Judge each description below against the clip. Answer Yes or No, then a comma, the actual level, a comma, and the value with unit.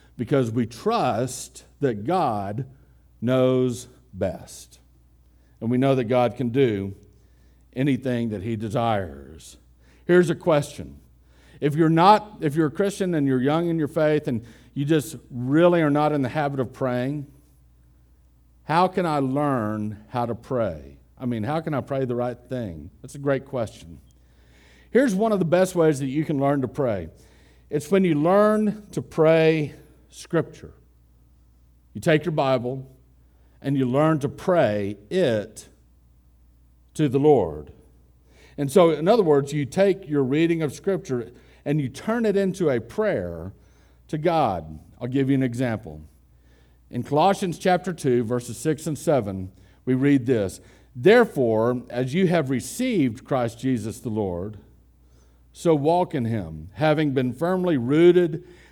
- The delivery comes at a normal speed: Yes, average, 155 wpm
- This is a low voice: Yes, low, 125 Hz